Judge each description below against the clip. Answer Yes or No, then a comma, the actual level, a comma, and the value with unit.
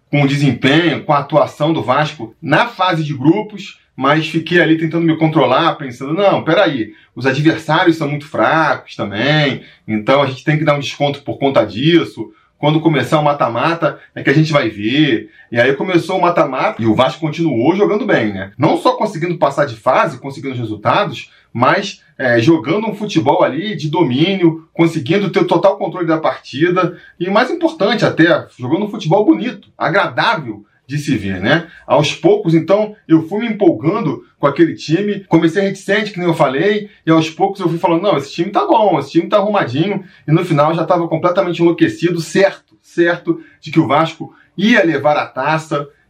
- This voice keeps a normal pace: No, fast, 190 wpm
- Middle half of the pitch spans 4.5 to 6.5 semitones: No, average, 4.0 semitones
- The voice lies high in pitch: No, medium, 160 Hz